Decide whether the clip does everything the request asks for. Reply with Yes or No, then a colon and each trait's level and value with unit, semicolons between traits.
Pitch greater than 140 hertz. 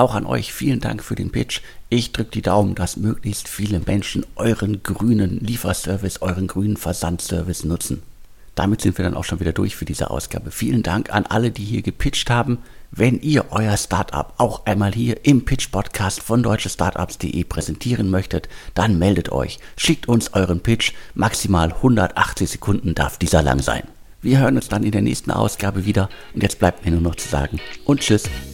No: low, 100 Hz